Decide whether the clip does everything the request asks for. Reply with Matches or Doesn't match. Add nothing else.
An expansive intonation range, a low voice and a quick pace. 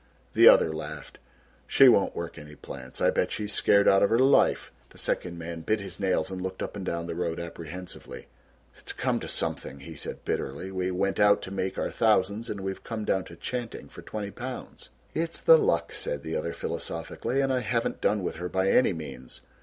Doesn't match